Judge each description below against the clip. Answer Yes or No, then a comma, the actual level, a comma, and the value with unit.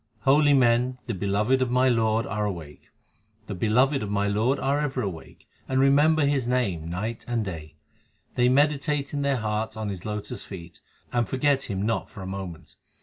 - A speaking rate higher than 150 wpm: Yes, average, 190 wpm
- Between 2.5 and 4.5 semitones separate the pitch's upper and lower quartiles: No, average, 4.9 semitones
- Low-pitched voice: Yes, low, 115 Hz